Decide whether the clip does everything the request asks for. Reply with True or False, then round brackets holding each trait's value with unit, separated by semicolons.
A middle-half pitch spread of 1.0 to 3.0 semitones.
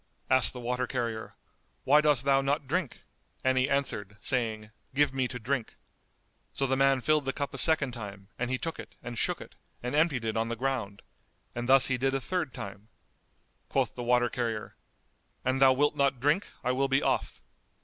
True (2.5 semitones)